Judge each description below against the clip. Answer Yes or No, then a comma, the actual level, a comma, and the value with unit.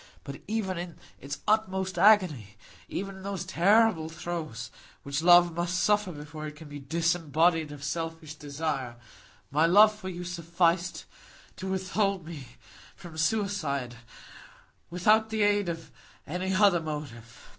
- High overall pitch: No, medium, 170 Hz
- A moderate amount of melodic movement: Yes, average, 4.1 semitones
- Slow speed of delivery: Yes, slow, 130 wpm